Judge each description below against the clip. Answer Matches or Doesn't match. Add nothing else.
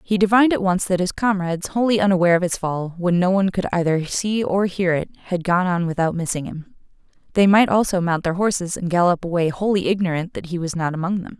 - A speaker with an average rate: Doesn't match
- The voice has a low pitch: Doesn't match